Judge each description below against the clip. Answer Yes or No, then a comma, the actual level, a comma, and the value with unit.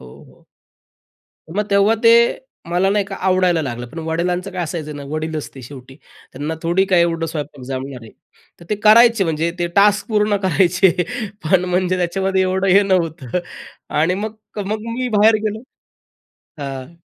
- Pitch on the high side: No, medium, 180 Hz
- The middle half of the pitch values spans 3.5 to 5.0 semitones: Yes, average, 4.1 semitones